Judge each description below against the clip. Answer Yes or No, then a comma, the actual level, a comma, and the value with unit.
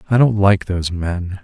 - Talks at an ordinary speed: No, fast, 210 wpm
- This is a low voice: Yes, low, 100 Hz